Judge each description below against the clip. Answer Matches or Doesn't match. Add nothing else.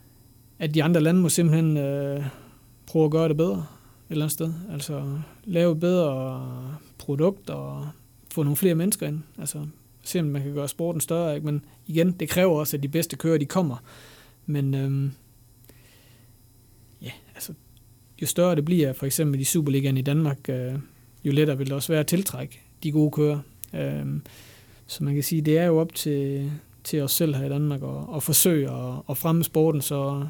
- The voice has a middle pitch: Matches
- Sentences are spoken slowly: Doesn't match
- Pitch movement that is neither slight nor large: Matches